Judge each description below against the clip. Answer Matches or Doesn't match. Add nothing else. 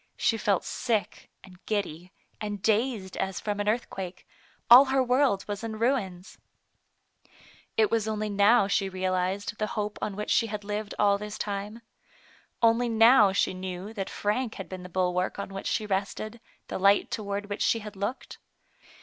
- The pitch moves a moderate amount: Doesn't match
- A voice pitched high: Matches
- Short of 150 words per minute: Doesn't match